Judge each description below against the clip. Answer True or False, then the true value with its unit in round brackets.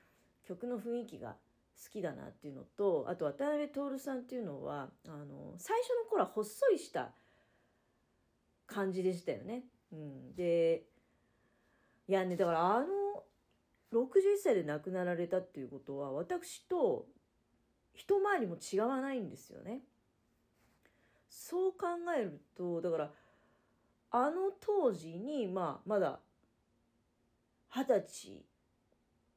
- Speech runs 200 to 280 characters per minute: True (225 characters per minute)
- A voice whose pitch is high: True (230 Hz)